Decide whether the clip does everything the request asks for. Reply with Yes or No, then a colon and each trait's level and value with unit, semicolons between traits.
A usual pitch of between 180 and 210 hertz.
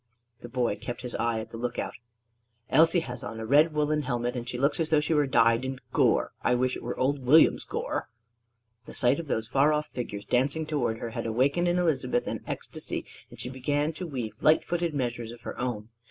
No: low, 130 Hz